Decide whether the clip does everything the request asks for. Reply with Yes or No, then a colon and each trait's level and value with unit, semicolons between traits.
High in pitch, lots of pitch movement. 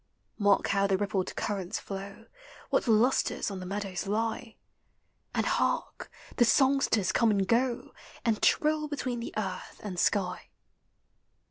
No: high, 210 Hz; average, 3.5 semitones